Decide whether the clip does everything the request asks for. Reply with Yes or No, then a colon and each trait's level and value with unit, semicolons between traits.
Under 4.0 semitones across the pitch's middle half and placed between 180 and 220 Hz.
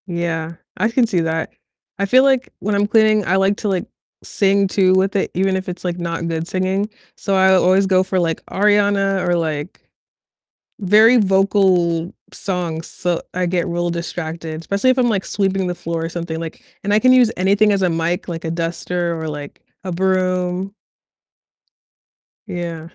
Yes: average, 2.7 semitones; medium, 185 Hz